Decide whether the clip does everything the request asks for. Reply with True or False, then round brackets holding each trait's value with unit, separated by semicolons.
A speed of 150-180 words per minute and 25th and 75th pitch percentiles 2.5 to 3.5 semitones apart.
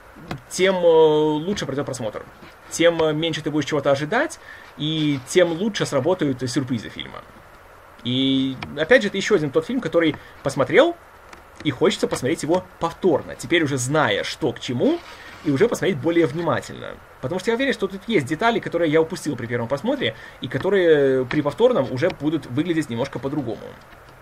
False (160 wpm; 4.6 semitones)